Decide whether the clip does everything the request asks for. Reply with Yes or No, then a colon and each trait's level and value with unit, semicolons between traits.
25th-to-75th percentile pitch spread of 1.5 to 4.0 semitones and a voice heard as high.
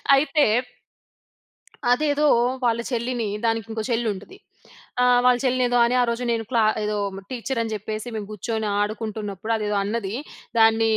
Yes: narrow, 2.4 semitones; high, 230 Hz